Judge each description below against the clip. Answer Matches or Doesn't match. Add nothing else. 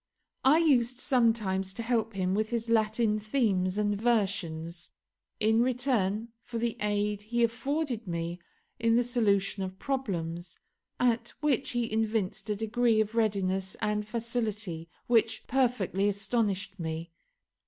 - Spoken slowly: Matches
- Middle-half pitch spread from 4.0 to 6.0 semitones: Doesn't match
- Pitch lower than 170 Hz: Doesn't match